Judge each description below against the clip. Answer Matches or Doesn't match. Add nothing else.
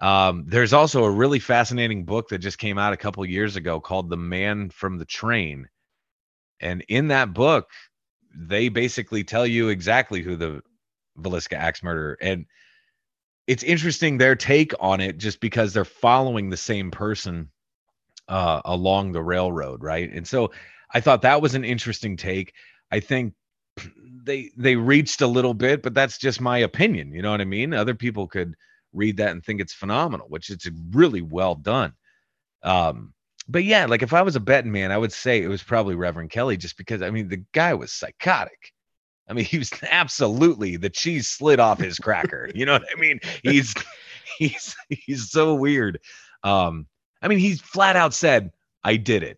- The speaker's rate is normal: Matches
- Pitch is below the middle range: Matches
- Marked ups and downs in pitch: Matches